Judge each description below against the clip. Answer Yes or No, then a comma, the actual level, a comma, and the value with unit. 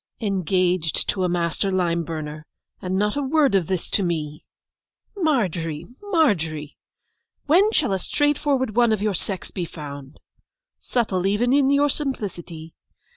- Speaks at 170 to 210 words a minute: No, average, 140 wpm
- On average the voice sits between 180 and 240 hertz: Yes, high, 190 Hz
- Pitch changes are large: Yes, wide, 7.7 semitones